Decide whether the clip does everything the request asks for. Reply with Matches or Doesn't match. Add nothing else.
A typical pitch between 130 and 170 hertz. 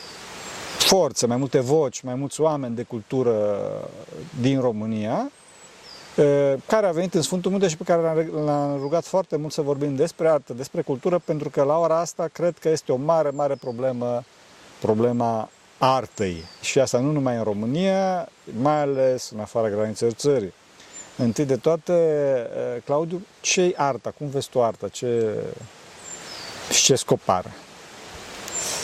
Matches